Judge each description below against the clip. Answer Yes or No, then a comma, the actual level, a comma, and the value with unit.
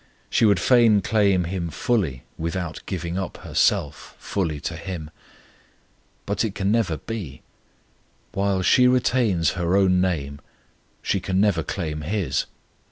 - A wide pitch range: No, average, 3.6 semitones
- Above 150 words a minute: No, slow, 135 wpm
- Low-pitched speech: Yes, very low, 95 Hz